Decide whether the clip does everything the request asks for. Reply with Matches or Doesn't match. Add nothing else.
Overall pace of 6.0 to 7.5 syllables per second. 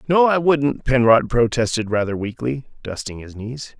Doesn't match